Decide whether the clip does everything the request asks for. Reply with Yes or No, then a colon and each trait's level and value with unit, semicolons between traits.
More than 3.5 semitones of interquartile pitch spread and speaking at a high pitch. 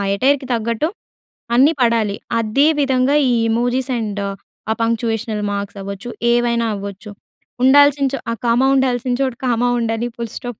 No: average, 2.8 semitones; high, 235 Hz